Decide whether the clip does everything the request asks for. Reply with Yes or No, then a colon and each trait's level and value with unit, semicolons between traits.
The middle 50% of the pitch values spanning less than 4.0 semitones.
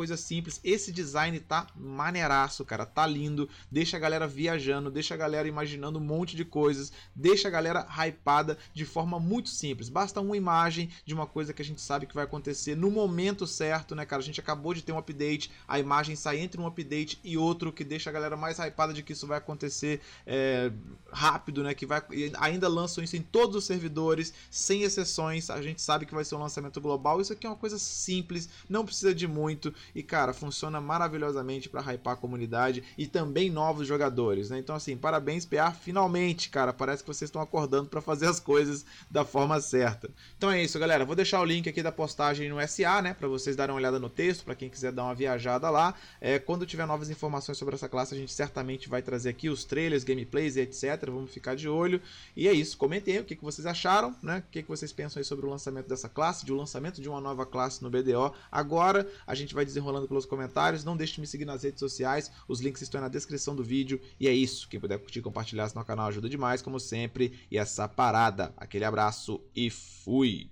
Yes: average, 3.6 semitones